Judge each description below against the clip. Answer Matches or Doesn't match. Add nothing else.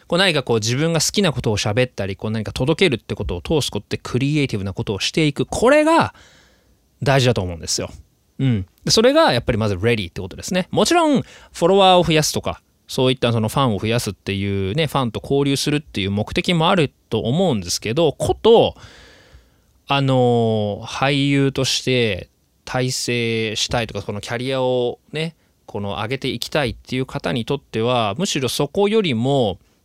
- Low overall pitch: Matches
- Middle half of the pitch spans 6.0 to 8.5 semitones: Doesn't match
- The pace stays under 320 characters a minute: Doesn't match